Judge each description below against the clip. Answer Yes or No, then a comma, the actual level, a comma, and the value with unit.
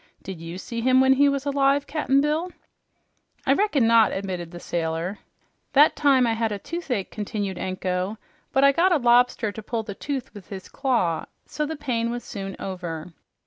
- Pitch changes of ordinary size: No, wide, 6.4 semitones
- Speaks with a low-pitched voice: No, high, 230 Hz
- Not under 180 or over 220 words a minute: Yes, average, 185 wpm